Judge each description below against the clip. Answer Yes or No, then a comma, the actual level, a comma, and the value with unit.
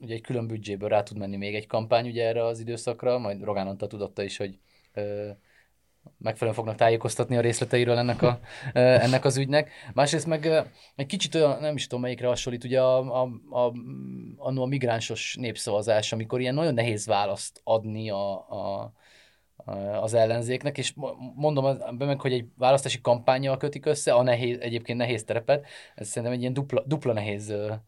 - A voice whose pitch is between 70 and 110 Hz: No, low, 120 Hz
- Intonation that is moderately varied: Yes, average, 3.1 semitones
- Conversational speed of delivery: No, fast, 180 wpm